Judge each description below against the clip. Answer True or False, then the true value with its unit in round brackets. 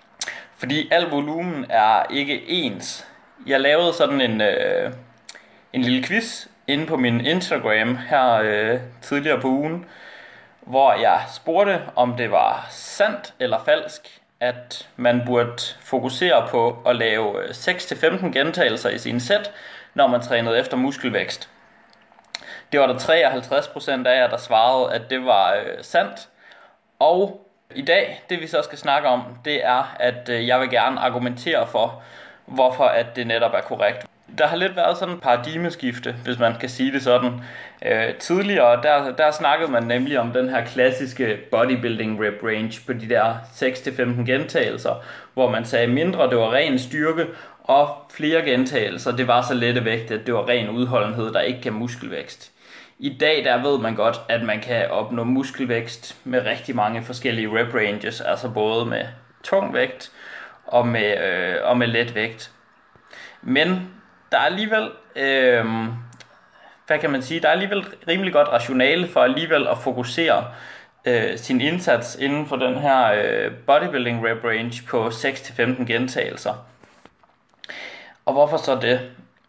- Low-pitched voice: True (125 Hz)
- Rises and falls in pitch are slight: False (3.7 semitones)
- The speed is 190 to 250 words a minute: False (155 wpm)